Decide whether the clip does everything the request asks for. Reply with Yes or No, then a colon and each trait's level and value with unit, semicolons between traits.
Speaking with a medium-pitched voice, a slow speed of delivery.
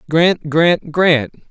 Yes: medium, 160 Hz; slow, 120 wpm